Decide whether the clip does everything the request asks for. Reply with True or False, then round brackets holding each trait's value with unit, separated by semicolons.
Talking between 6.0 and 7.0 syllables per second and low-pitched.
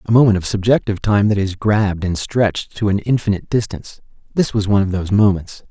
True (6.5 syllables/s; 100 Hz)